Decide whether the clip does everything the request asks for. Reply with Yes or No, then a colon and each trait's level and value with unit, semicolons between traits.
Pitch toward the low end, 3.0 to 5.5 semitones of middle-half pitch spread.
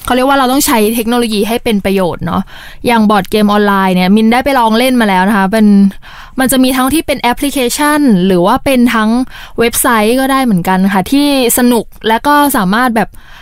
No: high, 235 Hz; average, 3.9 semitones